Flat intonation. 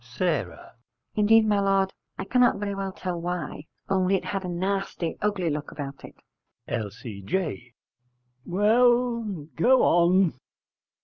No: average, 3.9 semitones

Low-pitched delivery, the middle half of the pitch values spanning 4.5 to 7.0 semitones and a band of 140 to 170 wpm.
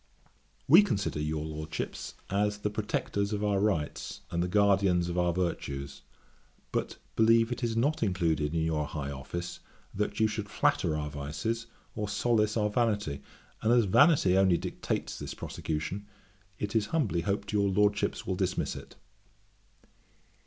Yes: low, 100 Hz; average, 4.8 semitones; average, 150 wpm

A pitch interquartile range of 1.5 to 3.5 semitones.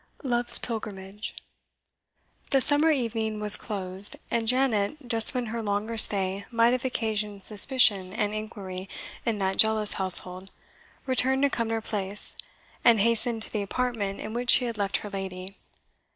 Yes: average, 3.0 semitones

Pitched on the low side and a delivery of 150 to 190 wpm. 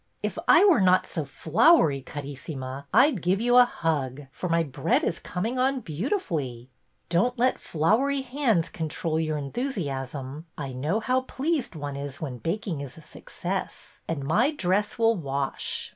No: medium, 165 Hz; average, 170 wpm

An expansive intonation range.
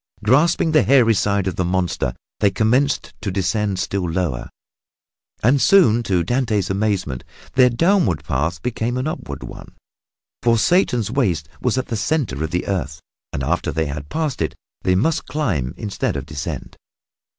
Yes: wide, 6.8 semitones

